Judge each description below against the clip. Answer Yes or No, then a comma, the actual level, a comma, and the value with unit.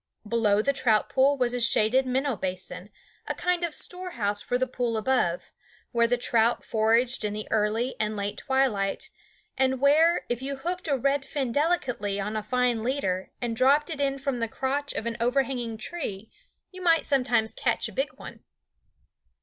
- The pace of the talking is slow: No, average, 180 wpm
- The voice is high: Yes, high, 245 Hz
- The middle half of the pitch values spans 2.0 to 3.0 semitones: No, average, 4.1 semitones